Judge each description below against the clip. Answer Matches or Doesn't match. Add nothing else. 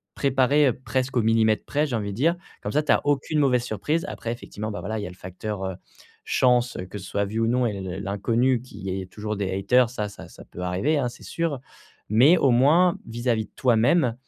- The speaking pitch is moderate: Doesn't match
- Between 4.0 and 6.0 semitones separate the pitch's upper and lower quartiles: Matches